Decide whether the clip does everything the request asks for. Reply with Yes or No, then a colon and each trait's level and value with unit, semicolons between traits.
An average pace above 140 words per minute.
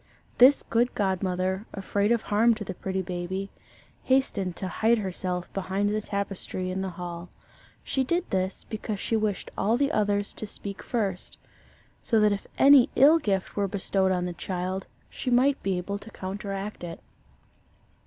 Yes: average, 165 wpm